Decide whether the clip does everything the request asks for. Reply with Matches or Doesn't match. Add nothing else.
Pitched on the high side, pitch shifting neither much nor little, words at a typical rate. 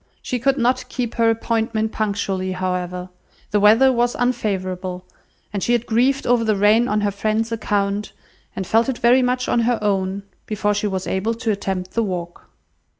Matches